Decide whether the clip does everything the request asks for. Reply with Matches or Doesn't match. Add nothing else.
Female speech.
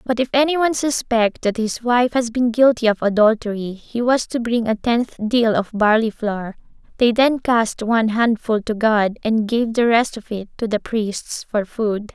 Matches